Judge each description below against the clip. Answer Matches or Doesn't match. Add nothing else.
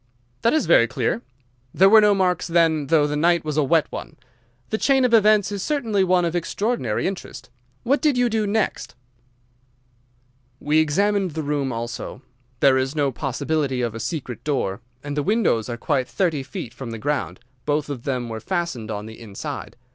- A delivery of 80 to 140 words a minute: Doesn't match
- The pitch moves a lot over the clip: Matches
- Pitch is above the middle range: Doesn't match